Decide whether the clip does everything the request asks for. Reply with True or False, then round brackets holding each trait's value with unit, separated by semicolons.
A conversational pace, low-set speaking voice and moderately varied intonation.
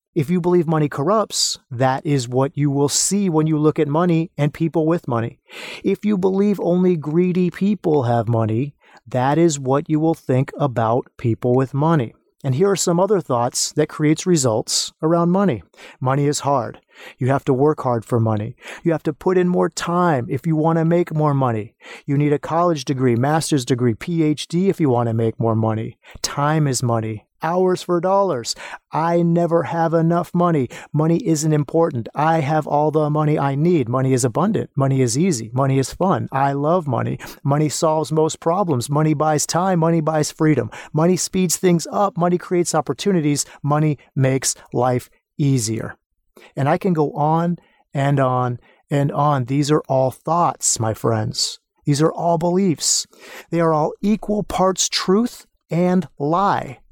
False (180 wpm; 155 Hz; 4.2 semitones)